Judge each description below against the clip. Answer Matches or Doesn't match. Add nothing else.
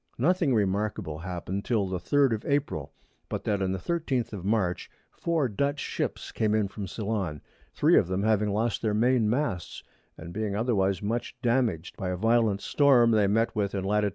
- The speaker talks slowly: Doesn't match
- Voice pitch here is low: Matches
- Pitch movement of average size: Matches